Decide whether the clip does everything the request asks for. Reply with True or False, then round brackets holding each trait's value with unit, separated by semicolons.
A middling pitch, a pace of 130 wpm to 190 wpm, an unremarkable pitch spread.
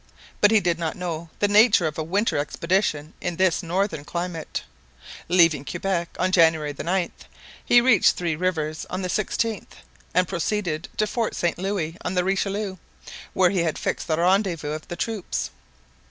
True (180 Hz; 170 wpm; 3.1 semitones)